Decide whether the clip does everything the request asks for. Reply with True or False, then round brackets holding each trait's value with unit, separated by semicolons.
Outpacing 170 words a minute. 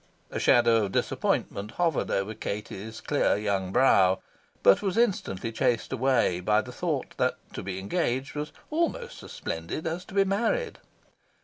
False (155 wpm)